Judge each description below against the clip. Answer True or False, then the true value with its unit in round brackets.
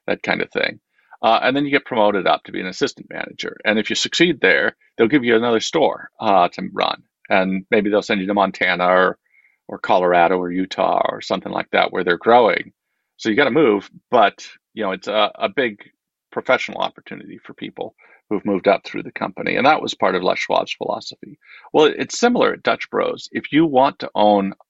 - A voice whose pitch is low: True (105 Hz)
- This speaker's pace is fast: True (220 wpm)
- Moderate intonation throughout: False (7.3 semitones)